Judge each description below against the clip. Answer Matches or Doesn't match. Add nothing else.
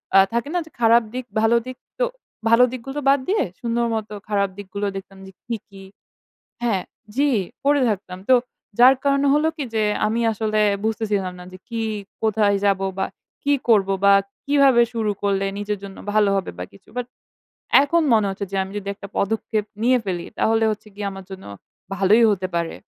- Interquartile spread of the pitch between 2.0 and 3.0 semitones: Doesn't match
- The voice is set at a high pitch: Matches